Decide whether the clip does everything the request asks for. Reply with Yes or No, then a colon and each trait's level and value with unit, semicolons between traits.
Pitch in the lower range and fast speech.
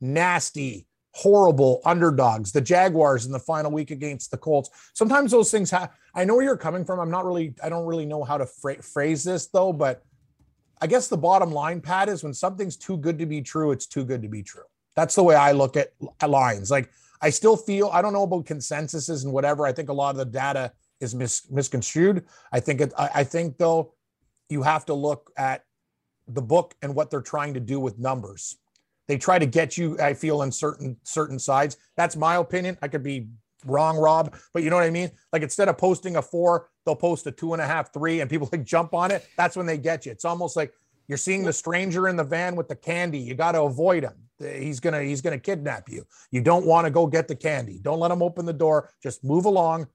No: medium, 155 Hz; fast, 235 wpm